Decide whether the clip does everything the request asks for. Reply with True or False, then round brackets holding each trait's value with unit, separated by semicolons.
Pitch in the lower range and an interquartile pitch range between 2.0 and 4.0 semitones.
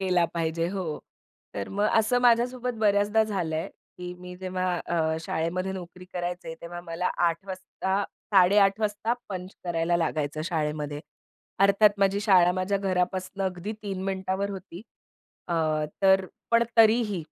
False (185 Hz; 2.6 semitones)